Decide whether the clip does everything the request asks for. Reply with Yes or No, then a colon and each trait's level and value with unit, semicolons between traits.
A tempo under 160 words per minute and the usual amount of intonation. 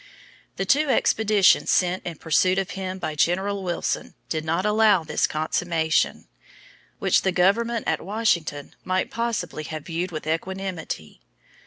Yes: average, 140 wpm; average, 3.7 semitones